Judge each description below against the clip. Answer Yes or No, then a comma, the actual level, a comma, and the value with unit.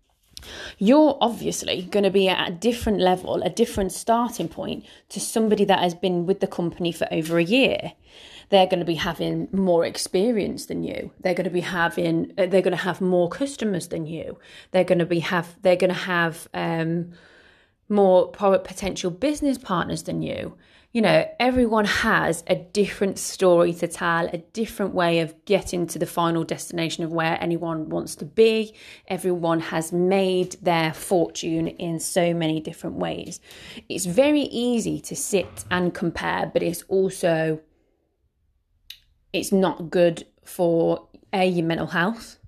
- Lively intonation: No, narrow, 2.6 semitones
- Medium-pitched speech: Yes, medium, 180 Hz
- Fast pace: No, average, 160 wpm